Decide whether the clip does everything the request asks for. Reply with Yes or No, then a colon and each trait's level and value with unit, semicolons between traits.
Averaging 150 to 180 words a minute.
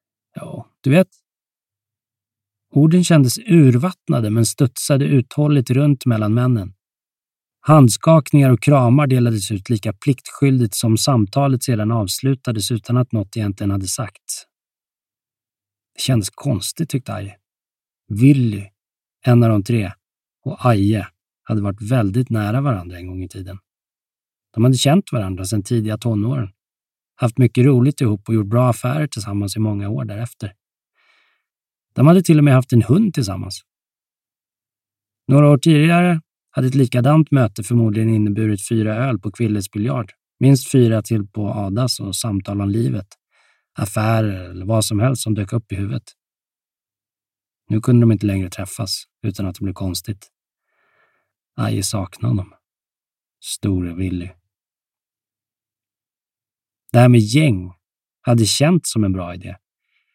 No: average, 140 wpm